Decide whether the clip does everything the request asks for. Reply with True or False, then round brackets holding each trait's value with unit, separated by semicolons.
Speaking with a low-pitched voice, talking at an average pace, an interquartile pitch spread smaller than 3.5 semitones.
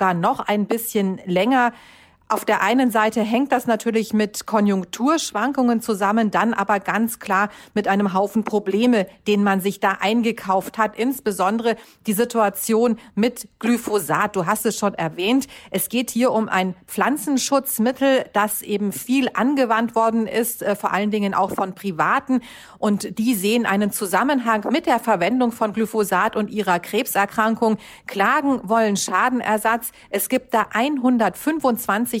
False (220 Hz; 140 wpm; 2.9 semitones)